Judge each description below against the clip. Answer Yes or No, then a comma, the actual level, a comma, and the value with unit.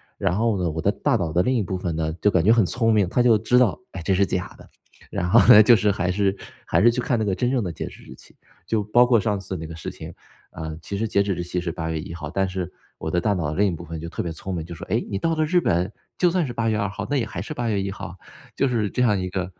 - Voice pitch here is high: No, low, 100 Hz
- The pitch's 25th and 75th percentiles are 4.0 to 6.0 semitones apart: Yes, average, 4.6 semitones